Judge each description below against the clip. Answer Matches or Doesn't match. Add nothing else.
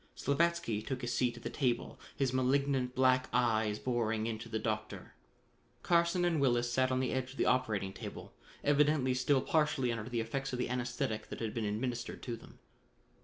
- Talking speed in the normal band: Matches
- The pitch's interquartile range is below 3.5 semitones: Matches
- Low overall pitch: Matches